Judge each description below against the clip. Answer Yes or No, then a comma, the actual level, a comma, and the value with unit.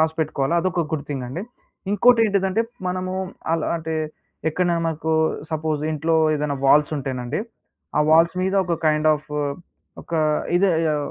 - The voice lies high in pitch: No, medium, 160 Hz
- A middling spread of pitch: Yes, average, 3.3 semitones